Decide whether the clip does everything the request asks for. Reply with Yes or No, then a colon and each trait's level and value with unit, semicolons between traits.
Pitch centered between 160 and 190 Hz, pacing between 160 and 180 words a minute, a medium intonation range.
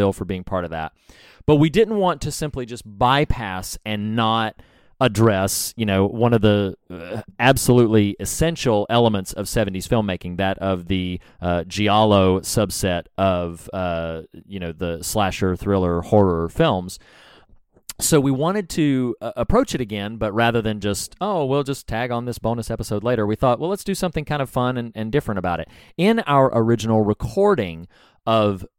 No: low, 110 Hz; average, 170 wpm; average, 4.7 semitones